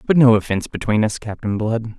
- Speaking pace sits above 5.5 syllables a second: Yes, 5.9 syllables/s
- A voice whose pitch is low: Yes, low, 110 Hz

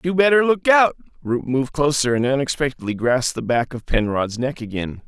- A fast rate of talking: No, average, 190 wpm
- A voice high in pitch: No, low, 135 Hz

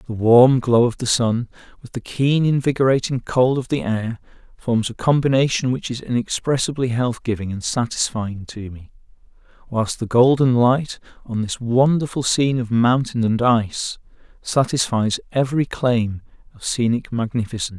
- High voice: No, low, 120 Hz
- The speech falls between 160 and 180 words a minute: No, average, 150 wpm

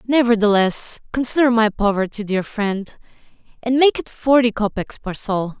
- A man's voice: No, female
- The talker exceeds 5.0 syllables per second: No, 4.7 syllables/s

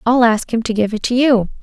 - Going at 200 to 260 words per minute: No, fast, 295 wpm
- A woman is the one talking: Yes, female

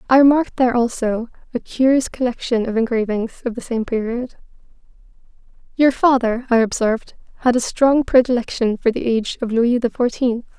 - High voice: Yes, high, 240 Hz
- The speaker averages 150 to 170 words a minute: Yes, average, 160 wpm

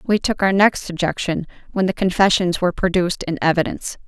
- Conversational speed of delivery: Yes, average, 175 wpm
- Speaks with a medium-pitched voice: Yes, medium, 180 Hz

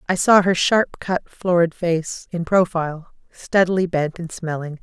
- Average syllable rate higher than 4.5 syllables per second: No, 4.4 syllables/s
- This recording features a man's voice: No, female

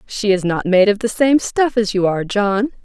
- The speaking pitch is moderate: No, high, 210 Hz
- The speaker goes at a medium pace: No, fast, 255 wpm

